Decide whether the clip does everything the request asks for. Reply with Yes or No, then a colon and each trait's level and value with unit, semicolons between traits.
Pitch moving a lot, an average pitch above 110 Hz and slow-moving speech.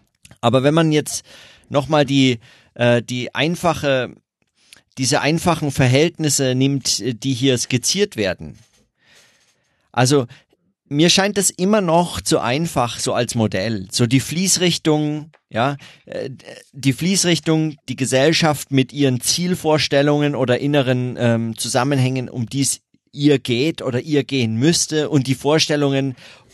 No: average, 3.4 semitones; medium, 140 Hz; slow, 120 wpm